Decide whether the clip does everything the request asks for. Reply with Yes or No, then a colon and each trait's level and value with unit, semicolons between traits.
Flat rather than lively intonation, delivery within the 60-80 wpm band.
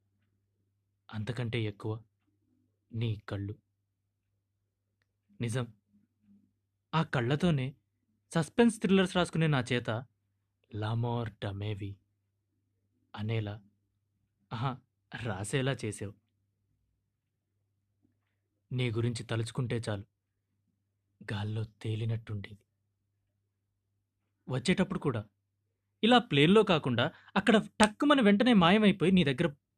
No: average, 4.1 semitones; slow, 70 wpm